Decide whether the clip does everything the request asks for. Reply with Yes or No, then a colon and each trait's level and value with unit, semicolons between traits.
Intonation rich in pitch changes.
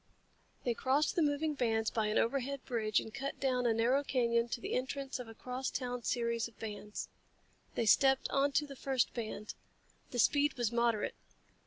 No: average, 3.0 semitones